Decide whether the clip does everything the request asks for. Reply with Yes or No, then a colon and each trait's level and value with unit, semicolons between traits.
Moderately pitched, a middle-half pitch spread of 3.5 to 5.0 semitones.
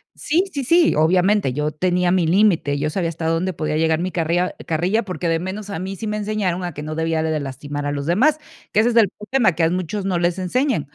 Yes: medium, 175 Hz; average, 4.5 semitones